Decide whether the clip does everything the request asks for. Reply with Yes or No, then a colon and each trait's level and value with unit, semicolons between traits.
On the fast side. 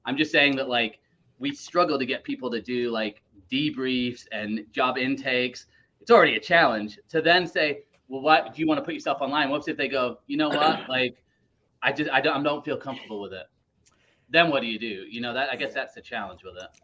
Yes: fast, 235 wpm